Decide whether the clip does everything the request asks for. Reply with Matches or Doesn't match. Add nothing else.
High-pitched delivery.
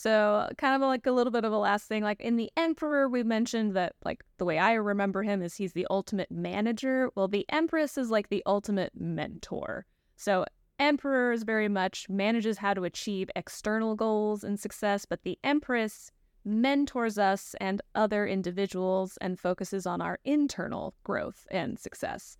Matches